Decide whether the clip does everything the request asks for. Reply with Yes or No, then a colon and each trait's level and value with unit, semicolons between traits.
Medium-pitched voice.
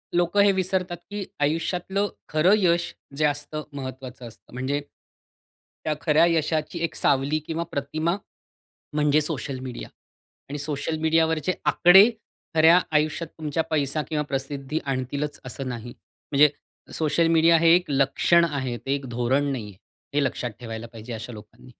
Yes: medium, 150 Hz